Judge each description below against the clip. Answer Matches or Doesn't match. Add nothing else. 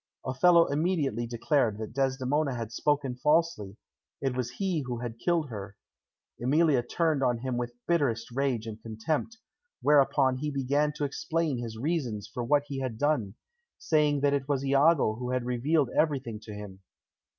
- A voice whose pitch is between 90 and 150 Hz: Matches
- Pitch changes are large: Doesn't match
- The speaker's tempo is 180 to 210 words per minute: Doesn't match